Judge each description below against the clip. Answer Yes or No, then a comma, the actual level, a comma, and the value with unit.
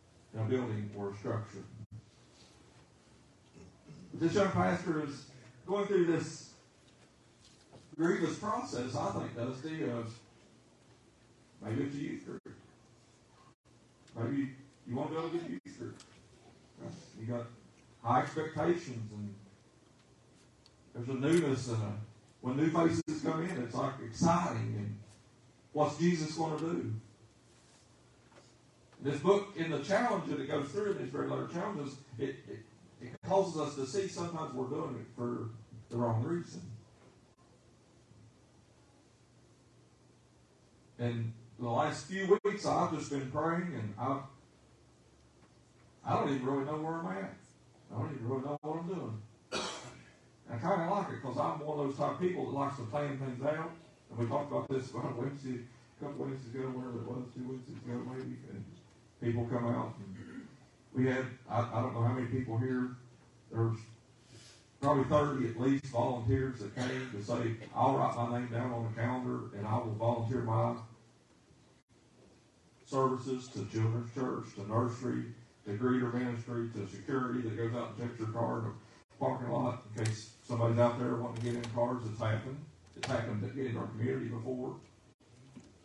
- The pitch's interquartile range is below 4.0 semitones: Yes, average, 3.6 semitones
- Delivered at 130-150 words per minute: No, average, 160 wpm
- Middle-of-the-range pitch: No, low, 125 Hz